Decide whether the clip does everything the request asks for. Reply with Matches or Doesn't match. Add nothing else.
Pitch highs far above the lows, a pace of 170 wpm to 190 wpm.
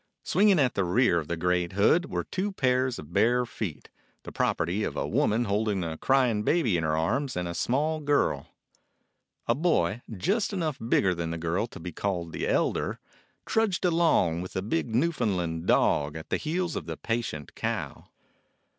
Matches